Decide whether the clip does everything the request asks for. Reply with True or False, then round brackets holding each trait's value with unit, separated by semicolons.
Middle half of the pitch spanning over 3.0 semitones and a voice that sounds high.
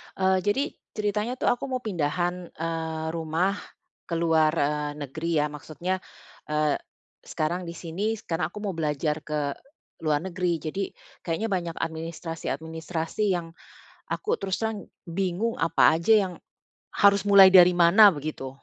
False (3.4 semitones; 170 Hz)